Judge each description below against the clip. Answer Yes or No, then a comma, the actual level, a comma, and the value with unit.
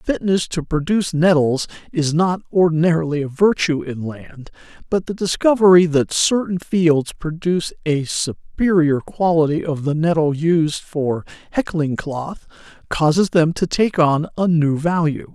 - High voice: No, medium, 160 Hz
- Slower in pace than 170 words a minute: Yes, average, 140 wpm